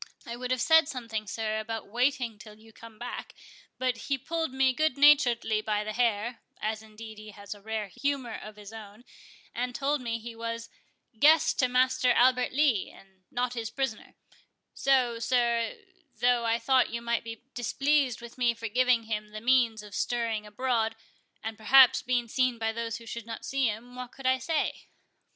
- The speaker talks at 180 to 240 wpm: Yes, average, 185 wpm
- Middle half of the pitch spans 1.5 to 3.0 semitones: Yes, narrow, 2.6 semitones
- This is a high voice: Yes, high, 235 Hz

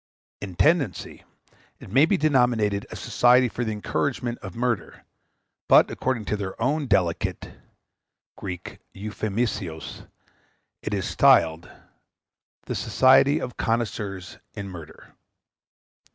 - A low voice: Yes, low, 110 Hz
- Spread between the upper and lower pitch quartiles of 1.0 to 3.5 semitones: No, average, 4.7 semitones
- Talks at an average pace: No, slow, 110 wpm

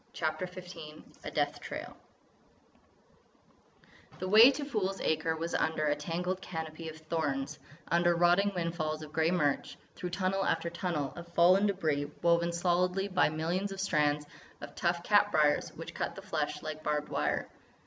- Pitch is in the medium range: Yes, medium, 170 Hz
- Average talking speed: Yes, average, 160 wpm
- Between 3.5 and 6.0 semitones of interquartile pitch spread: No, average, 2.8 semitones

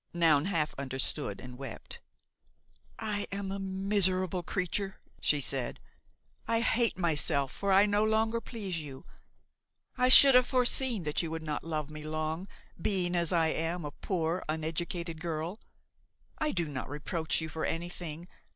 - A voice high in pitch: No, medium, 170 Hz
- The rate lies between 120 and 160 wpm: Yes, average, 150 wpm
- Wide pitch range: No, average, 4.3 semitones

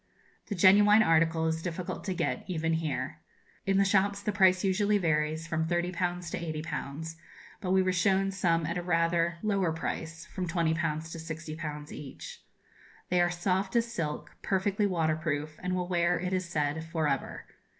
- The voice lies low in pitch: No, medium, 175 Hz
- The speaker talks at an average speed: Yes, average, 170 wpm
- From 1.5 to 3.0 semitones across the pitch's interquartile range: Yes, average, 2.7 semitones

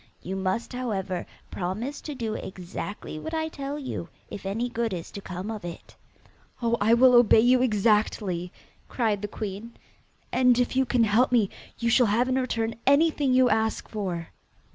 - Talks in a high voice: Yes, high, 225 Hz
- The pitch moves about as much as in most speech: Yes, average, 4.2 semitones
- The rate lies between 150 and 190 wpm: Yes, average, 175 wpm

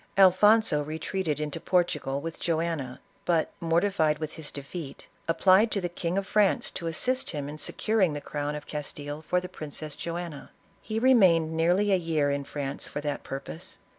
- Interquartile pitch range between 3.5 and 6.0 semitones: Yes, average, 3.9 semitones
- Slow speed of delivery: No, average, 170 wpm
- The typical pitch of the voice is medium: Yes, medium, 165 Hz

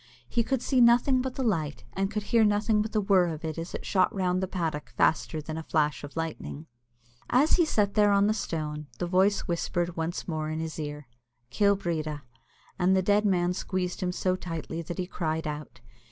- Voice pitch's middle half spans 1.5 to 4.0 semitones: No, average, 4.4 semitones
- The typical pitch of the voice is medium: Yes, medium, 180 Hz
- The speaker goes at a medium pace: No, fast, 215 wpm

